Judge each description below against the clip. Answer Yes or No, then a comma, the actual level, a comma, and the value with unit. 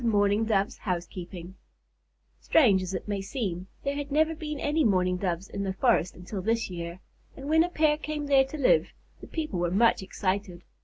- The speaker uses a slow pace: No, average, 190 wpm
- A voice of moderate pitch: No, high, 205 Hz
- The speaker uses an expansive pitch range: Yes, wide, 7.5 semitones